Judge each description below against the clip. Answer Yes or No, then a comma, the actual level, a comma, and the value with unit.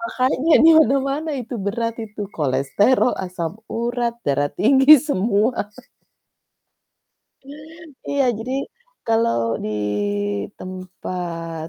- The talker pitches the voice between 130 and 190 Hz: No, high, 225 Hz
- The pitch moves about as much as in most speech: No, wide, 6.3 semitones